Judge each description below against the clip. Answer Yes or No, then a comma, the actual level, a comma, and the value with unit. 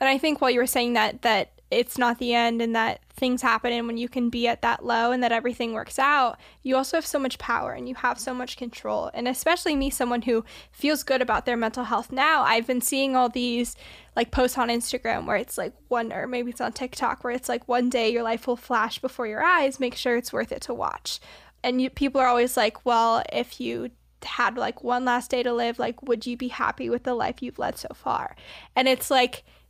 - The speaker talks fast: Yes, fast, 245 wpm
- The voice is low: No, high, 245 Hz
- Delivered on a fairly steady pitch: Yes, narrow, 1.6 semitones